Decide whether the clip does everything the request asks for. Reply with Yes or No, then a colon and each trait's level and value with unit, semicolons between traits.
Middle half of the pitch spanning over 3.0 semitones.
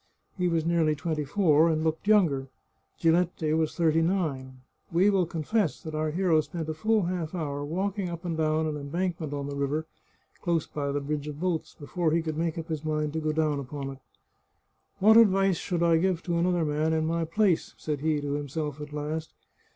No: narrow, 2.5 semitones